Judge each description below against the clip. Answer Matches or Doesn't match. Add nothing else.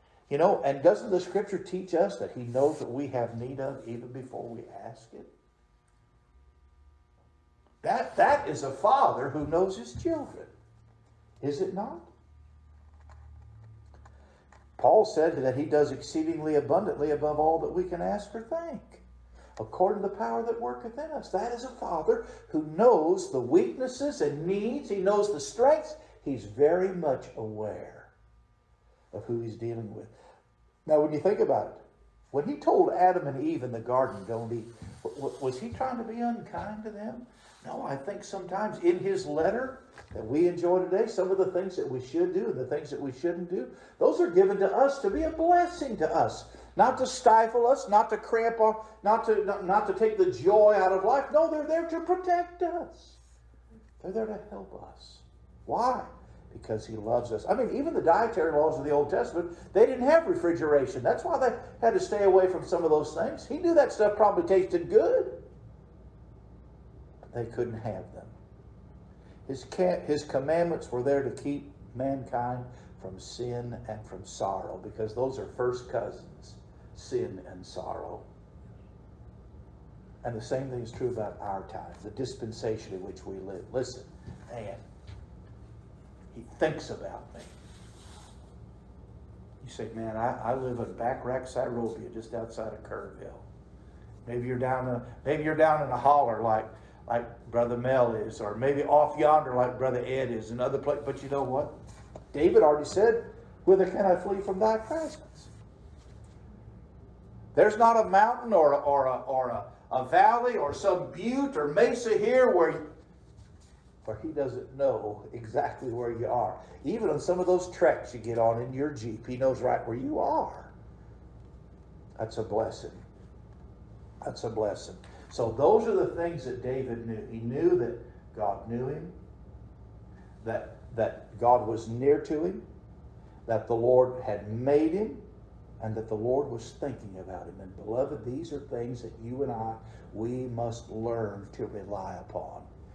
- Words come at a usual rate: Matches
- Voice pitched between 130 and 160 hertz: Matches